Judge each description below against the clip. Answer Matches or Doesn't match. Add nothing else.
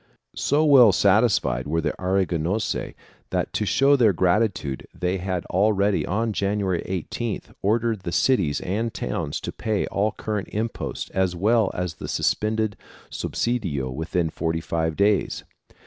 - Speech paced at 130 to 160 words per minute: Matches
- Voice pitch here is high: Doesn't match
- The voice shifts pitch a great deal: Doesn't match